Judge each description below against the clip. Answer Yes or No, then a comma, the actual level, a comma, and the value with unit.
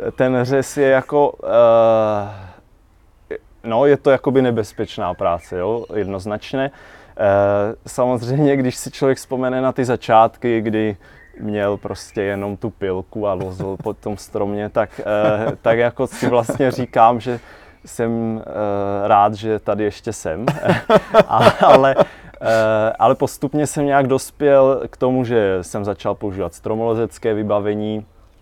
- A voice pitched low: Yes, low, 110 Hz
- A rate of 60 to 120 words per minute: No, average, 135 wpm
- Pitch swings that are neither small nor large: Yes, average, 3.9 semitones